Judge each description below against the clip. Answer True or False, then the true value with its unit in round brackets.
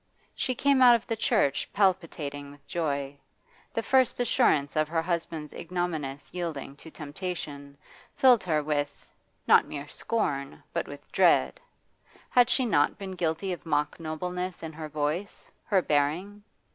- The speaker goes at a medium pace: True (145 wpm)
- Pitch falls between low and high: True (165 Hz)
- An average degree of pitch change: True (5.0 semitones)